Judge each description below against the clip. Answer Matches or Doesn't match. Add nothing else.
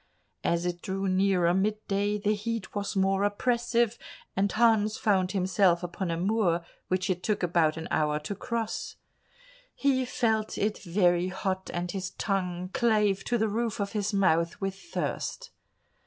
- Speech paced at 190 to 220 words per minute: Doesn't match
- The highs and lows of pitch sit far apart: Doesn't match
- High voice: Matches